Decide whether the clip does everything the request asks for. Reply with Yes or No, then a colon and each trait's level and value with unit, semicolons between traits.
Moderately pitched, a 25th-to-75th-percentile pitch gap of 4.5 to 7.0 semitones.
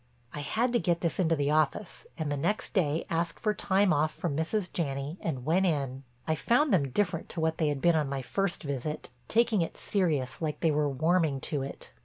No: medium, 160 Hz; average, 4.1 semitones